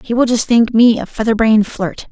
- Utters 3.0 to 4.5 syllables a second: No, 5.5 syllables/s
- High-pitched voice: Yes, high, 225 Hz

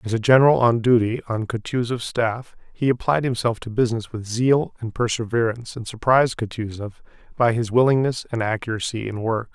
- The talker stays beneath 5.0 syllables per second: No, 5.6 syllables/s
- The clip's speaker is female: No, male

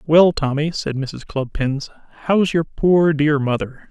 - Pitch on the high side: No, medium, 150 Hz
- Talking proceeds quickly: No, average, 155 wpm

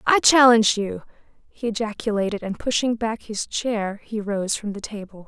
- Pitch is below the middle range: No, high, 215 Hz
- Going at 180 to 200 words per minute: No, average, 170 wpm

